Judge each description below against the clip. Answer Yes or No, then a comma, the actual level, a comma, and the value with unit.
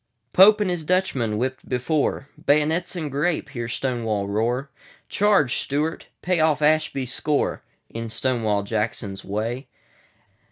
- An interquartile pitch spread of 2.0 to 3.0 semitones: No, average, 5.3 semitones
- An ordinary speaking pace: No, slow, 105 wpm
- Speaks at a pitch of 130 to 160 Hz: Yes, low, 135 Hz